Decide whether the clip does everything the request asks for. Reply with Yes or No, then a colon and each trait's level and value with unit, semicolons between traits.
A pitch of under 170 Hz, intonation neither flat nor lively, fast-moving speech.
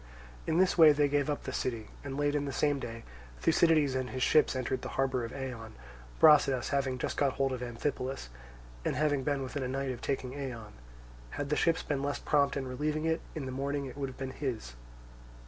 No: low, 135 Hz; narrow, 2.1 semitones; fast, 215 wpm